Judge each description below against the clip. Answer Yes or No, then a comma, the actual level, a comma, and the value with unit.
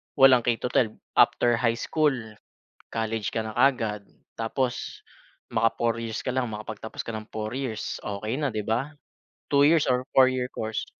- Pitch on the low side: Yes, low, 115 Hz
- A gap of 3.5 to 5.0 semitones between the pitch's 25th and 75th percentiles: No, average, 2.8 semitones